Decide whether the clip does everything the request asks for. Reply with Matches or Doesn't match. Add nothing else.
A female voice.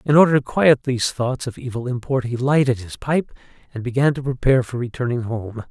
Doesn't match